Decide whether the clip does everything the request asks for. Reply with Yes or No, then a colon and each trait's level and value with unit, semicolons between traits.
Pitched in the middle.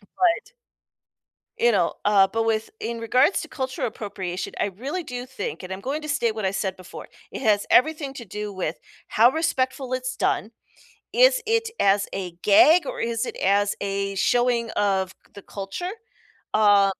No: high, 230 Hz